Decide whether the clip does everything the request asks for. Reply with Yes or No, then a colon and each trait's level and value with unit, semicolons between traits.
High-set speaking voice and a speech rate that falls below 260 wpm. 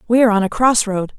No: high, 220 Hz; fast, 305 wpm